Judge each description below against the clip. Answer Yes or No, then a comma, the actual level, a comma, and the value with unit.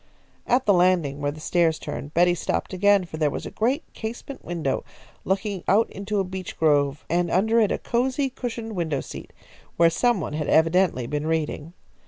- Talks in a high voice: No, medium, 175 Hz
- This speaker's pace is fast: No, average, 190 wpm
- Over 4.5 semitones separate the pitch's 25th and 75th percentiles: Yes, average, 5.2 semitones